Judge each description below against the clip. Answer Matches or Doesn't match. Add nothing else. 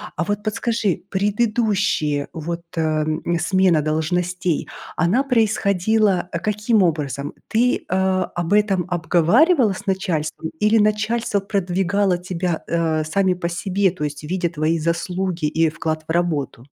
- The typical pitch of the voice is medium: Matches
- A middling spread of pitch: Matches